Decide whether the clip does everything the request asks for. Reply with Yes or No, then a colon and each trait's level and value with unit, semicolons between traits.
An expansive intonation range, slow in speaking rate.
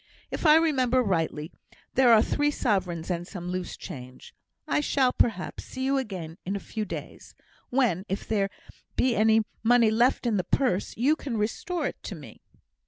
No: wide, 6.0 semitones; average, 175 wpm